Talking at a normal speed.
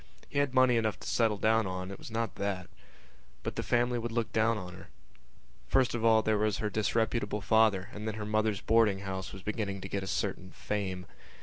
No: fast, 215 wpm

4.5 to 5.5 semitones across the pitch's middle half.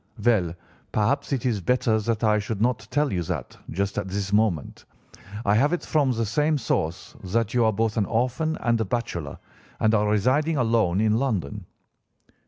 No: average, 3.8 semitones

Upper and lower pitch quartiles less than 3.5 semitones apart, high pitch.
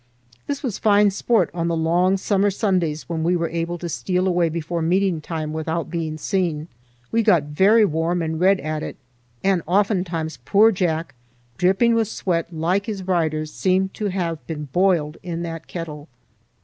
No: average, 3.1 semitones; medium, 175 Hz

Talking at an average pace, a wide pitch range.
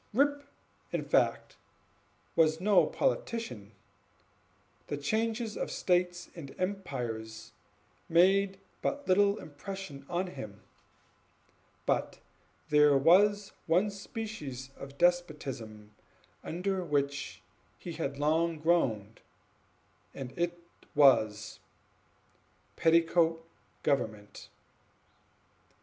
No: slow, 85 wpm; wide, 5.9 semitones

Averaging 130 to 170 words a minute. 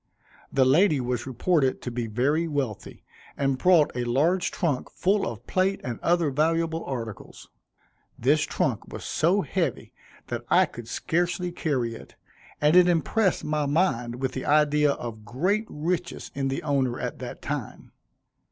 Yes: average, 155 wpm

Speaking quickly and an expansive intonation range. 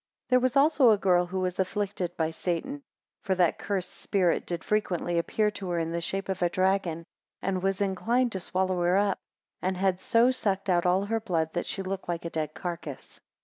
No: fast, 215 wpm; narrow, 2.5 semitones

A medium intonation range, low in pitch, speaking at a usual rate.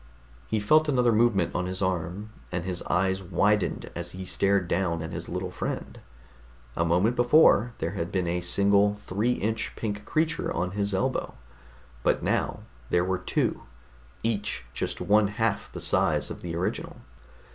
Yes: average, 3.4 semitones; low, 100 Hz; average, 165 wpm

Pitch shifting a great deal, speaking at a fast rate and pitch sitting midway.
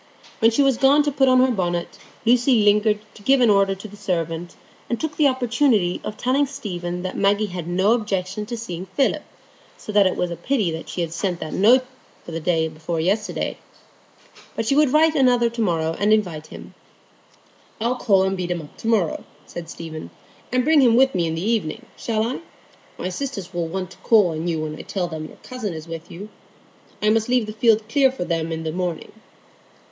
No: wide, 5.8 semitones; fast, 215 wpm; high, 205 Hz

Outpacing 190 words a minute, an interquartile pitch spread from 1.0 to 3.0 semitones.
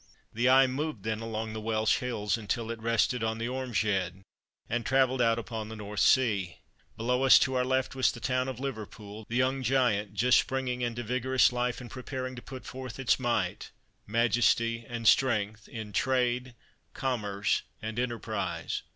No: average, 170 wpm; average, 2.7 semitones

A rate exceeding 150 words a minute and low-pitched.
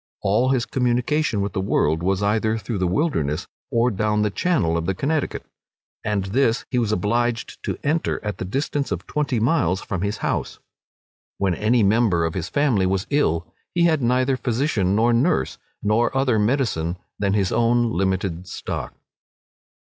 Yes: average, 170 wpm; low, 110 Hz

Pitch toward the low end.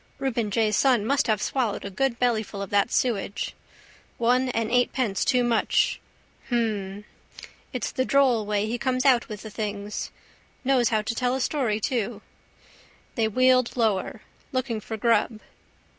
No: high, 230 Hz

